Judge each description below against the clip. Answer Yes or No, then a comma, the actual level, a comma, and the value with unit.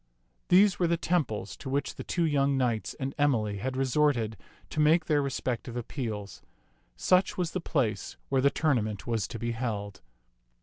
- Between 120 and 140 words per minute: No, average, 180 wpm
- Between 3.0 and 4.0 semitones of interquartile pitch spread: No, average, 5.2 semitones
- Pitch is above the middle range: No, low, 130 Hz